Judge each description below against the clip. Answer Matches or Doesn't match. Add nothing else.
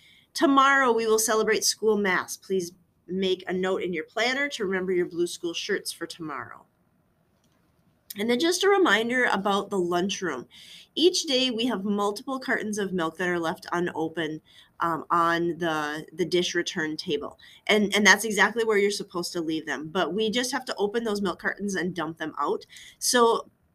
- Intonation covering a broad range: Doesn't match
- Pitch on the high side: Matches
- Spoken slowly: Doesn't match